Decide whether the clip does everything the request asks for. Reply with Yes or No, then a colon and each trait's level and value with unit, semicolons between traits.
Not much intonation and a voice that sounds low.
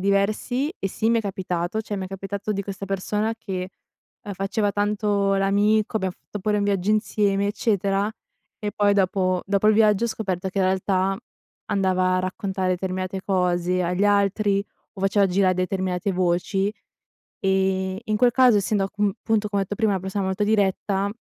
No: narrow, 1.7 semitones; high, 195 Hz